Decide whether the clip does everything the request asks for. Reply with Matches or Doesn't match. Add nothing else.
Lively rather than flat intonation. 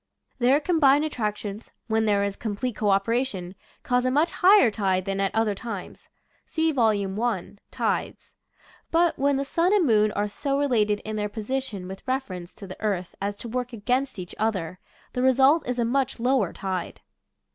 Doesn't match